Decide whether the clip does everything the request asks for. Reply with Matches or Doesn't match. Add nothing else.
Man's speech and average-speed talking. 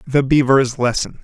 Matches